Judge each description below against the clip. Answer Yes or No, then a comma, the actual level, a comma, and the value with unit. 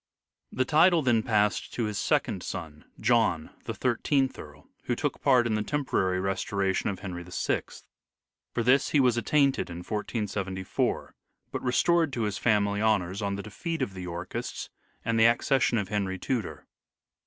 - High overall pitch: No, low, 105 Hz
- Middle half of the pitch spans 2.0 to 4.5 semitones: No, average, 4.9 semitones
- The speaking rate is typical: Yes, average, 170 wpm